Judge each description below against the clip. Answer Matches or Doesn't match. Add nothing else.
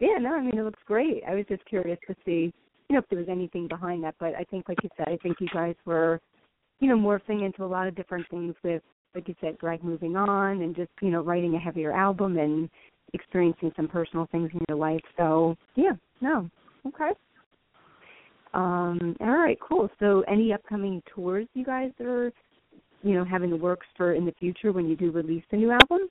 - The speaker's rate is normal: Doesn't match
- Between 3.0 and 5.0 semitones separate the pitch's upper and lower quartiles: Matches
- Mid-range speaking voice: Matches